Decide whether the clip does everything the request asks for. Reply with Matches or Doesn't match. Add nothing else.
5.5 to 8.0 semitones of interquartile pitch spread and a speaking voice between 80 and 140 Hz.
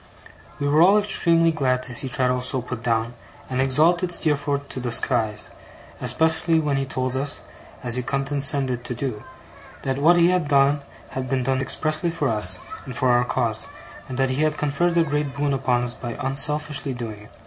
Doesn't match